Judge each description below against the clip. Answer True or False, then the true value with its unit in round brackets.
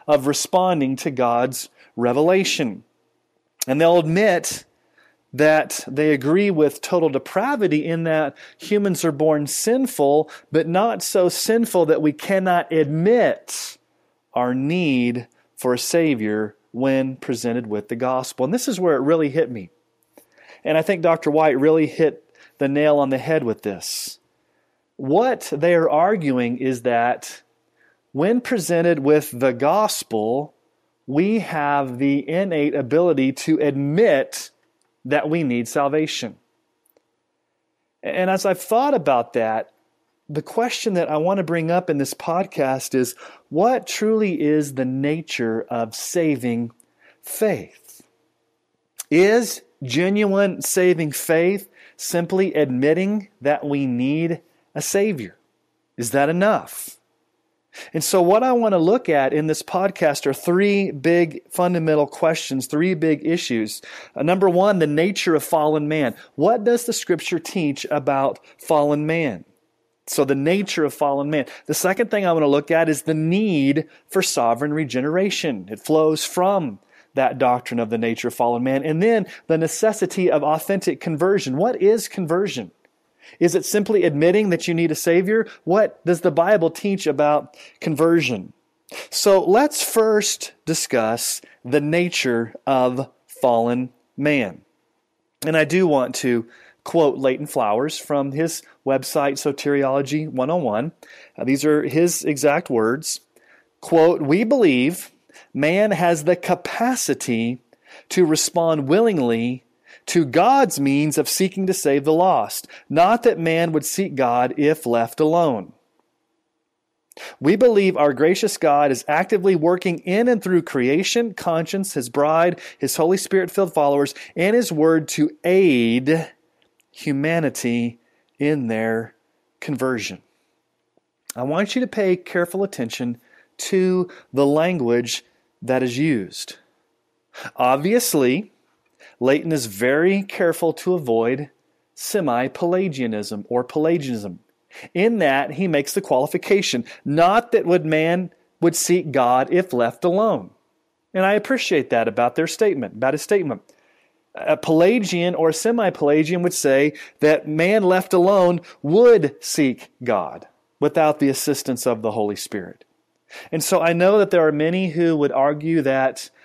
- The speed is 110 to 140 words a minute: True (135 wpm)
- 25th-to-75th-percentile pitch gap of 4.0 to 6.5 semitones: True (4.7 semitones)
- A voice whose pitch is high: False (160 Hz)